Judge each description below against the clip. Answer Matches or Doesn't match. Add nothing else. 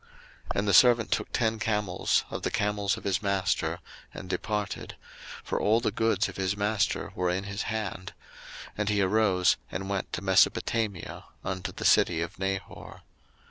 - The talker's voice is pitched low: Matches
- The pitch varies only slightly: Matches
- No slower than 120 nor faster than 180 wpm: Matches